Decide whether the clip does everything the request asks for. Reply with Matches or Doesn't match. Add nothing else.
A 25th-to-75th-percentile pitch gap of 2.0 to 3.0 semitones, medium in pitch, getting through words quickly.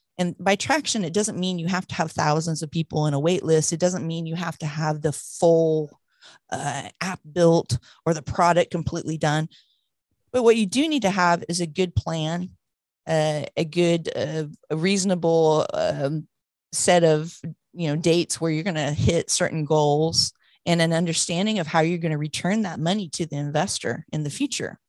Doesn't match